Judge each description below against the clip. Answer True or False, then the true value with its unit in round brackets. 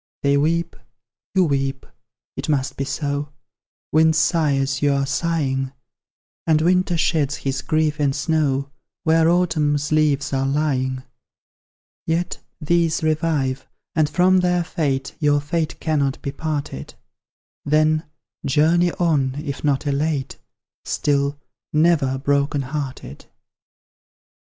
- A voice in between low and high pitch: True (150 Hz)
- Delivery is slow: True (120 wpm)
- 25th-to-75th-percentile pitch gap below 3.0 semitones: True (2.6 semitones)